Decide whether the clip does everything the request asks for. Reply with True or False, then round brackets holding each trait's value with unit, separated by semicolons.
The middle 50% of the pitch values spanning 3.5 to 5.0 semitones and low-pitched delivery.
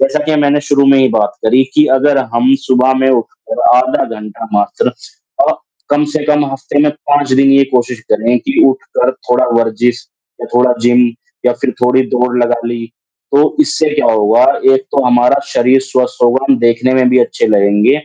False (3.0 semitones; 125 Hz)